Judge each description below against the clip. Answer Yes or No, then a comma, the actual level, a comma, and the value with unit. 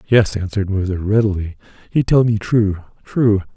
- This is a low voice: Yes, low, 105 Hz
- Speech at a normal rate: Yes, average, 150 wpm